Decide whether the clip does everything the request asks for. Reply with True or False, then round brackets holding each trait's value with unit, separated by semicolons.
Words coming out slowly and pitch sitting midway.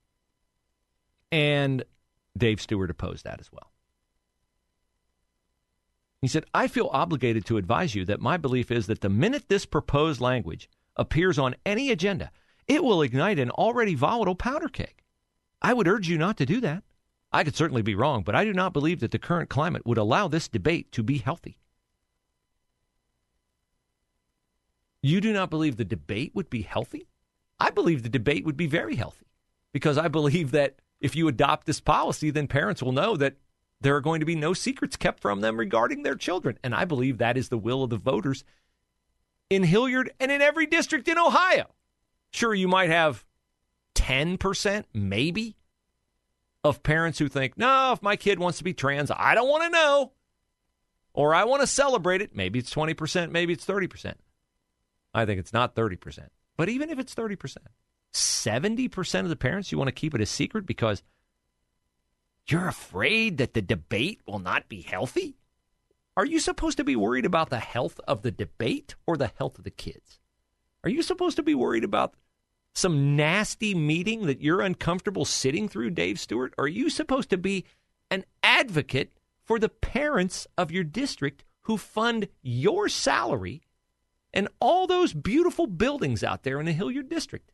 False (175 wpm; 155 Hz)